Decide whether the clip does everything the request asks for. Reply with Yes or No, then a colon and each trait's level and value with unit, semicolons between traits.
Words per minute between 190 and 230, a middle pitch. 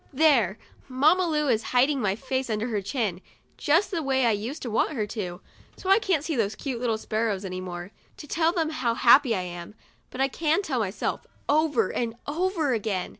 No: average, 200 wpm; high, 245 Hz